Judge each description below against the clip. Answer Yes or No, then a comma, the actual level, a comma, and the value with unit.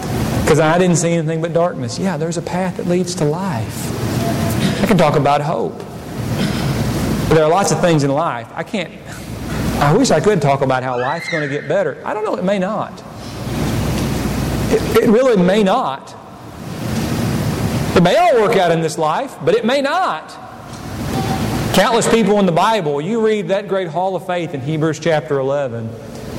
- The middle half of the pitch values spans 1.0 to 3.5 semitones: No, average, 4.7 semitones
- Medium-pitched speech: Yes, medium, 165 Hz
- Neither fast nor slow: Yes, average, 185 wpm